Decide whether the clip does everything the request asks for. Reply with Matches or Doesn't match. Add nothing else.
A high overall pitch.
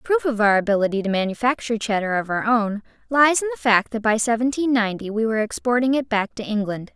Matches